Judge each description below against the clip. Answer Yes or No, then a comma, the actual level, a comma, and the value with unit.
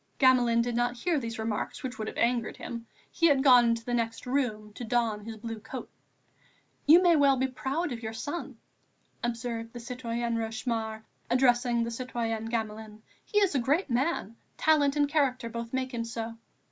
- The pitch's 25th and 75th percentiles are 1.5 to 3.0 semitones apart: Yes, narrow, 2.5 semitones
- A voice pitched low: No, high, 240 Hz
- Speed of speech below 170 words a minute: No, average, 185 wpm